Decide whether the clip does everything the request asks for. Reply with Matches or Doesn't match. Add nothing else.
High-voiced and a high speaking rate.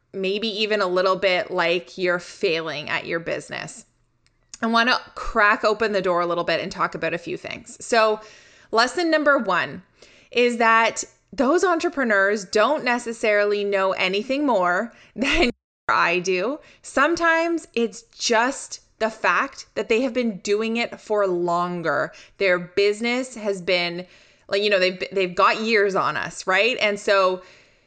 Doesn't match